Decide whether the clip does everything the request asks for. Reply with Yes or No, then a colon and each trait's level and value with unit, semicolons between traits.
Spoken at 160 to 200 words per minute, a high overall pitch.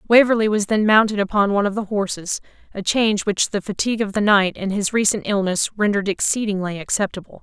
Yes: average, 195 wpm; high, 205 Hz